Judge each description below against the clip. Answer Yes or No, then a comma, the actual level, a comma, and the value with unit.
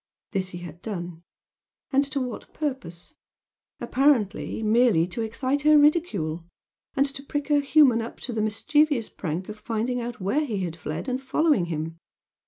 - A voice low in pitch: No, high, 230 Hz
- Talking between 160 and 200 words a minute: Yes, average, 165 wpm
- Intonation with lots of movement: Yes, wide, 7.4 semitones